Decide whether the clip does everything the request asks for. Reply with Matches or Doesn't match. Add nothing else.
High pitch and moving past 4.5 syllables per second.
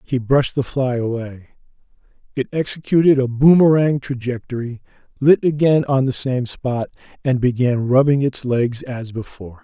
Doesn't match